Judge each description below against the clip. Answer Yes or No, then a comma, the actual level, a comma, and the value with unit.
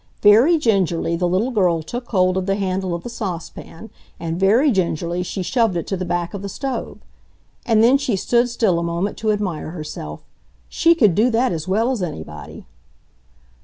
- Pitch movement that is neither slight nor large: Yes, average, 5.0 semitones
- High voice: Yes, high, 195 Hz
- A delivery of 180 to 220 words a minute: Yes, average, 190 wpm